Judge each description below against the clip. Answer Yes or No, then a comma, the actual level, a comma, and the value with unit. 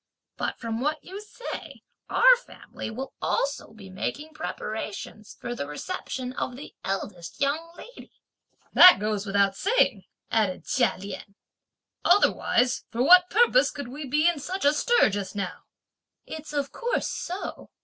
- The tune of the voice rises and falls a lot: Yes, wide, 8.7 semitones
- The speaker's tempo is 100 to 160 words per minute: Yes, average, 150 wpm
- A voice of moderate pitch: No, very high, 270 Hz